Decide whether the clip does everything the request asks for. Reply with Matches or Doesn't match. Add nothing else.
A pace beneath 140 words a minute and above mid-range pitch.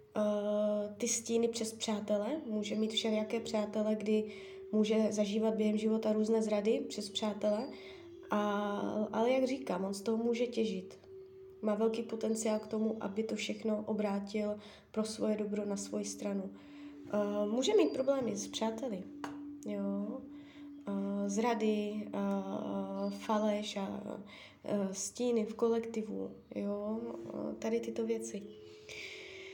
Matches